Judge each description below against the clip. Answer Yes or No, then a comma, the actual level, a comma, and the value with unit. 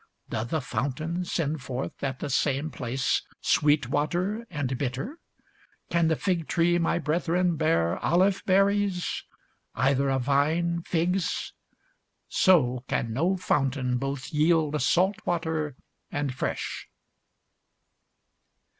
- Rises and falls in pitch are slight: No, average, 4.4 semitones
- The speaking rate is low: Yes, slow, 115 wpm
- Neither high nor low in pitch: Yes, medium, 155 Hz